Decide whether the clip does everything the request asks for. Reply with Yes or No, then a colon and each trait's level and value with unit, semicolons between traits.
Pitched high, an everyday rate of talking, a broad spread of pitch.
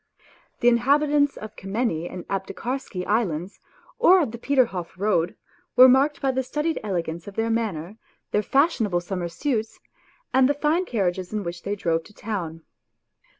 Yes: high, 215 Hz; average, 155 wpm; wide, 6.5 semitones